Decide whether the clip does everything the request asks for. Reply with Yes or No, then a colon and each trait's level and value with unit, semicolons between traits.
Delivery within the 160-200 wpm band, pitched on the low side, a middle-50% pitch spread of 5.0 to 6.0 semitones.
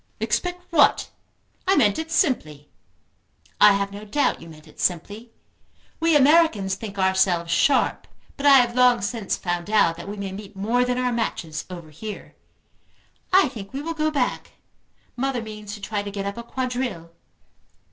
No: average, 170 wpm; high, 215 Hz; wide, 5.4 semitones